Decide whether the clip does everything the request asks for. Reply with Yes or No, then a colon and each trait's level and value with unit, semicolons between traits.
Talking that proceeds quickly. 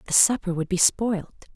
No: average, 195 wpm